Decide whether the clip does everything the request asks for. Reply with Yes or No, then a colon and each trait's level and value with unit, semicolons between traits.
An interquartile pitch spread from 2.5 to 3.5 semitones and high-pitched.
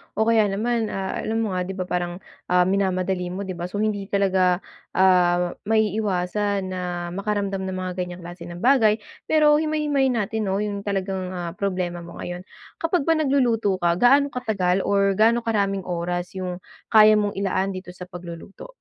Yes: average, 3.1 semitones; high, 195 Hz